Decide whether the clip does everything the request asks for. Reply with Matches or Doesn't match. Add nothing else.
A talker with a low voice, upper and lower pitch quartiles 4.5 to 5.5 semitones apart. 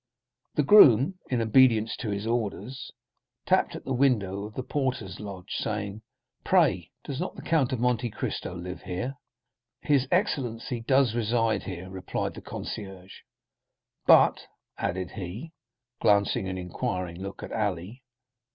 Matches